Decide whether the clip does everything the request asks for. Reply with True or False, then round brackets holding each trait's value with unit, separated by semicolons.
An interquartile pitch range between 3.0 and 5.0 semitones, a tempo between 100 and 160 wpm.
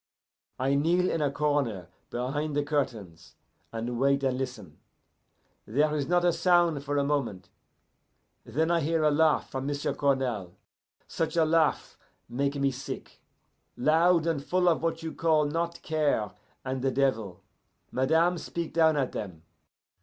True (3.6 semitones; 155 wpm)